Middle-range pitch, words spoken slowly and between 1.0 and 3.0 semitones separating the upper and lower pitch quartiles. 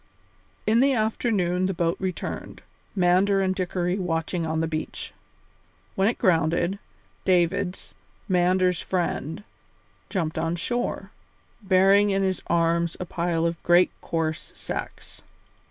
Yes: medium, 180 Hz; slow, 120 wpm; narrow, 2.4 semitones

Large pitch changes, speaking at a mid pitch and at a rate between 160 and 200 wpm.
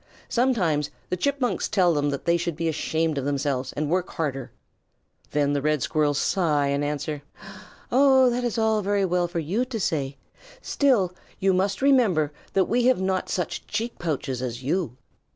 Yes: wide, 6.3 semitones; medium, 170 Hz; average, 175 wpm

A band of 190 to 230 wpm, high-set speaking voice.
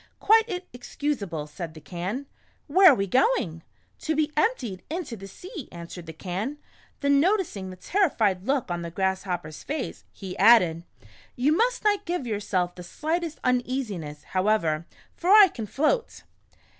No: average, 165 wpm; high, 235 Hz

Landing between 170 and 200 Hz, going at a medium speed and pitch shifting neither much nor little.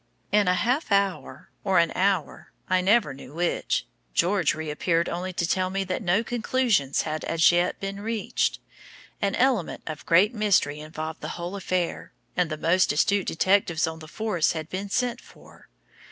Yes: medium, 185 Hz; average, 170 wpm; average, 3.7 semitones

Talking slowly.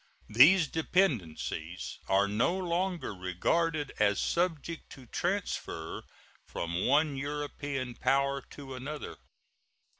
Yes: slow, 95 wpm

